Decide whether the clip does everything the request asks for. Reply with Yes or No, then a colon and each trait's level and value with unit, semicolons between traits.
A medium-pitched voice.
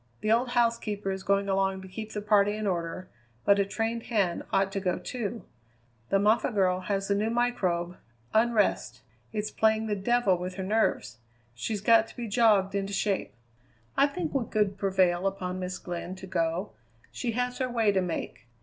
No: high, 200 Hz